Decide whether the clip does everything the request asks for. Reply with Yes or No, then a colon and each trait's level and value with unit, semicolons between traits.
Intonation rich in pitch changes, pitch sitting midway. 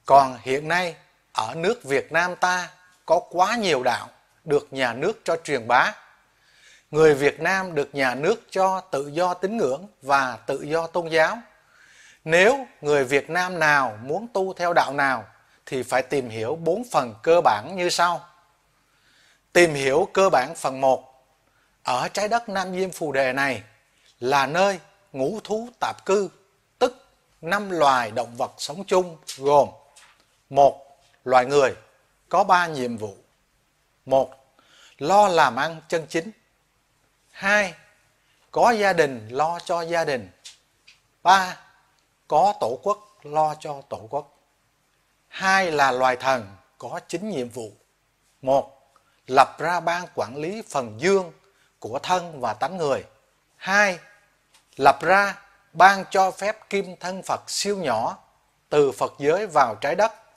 Yes: wide, 5.8 semitones; medium, 165 Hz